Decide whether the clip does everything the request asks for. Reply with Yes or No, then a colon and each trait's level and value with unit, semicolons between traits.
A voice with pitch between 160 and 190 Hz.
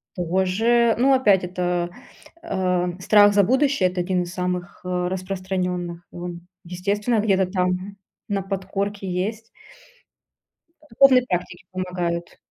Yes: medium, 185 Hz